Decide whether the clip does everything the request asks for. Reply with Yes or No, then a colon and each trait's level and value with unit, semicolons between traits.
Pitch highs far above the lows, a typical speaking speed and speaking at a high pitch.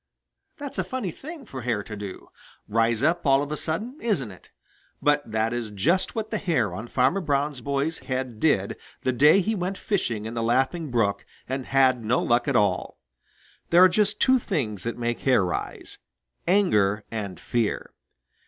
No: wide, 7.4 semitones; average, 180 wpm; low, 130 Hz